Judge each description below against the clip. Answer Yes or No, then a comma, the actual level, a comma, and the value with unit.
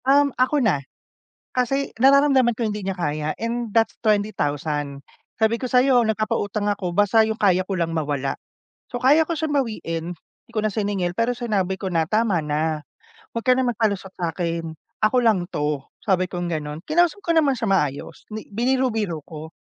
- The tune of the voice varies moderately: No, wide, 6.4 semitones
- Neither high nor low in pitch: No, high, 210 Hz